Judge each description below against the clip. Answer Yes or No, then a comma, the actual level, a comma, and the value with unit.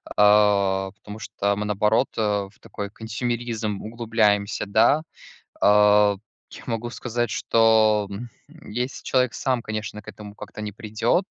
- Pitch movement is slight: Yes, narrow, 2.1 semitones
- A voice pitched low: Yes, low, 105 Hz